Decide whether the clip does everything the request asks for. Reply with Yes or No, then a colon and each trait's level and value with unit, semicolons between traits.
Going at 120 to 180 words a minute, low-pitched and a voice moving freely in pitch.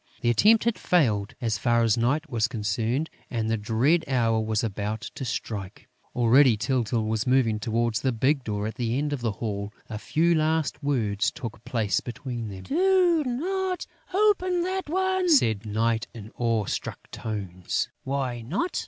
Yes: average, 170 wpm; low, 120 Hz; wide, 6.1 semitones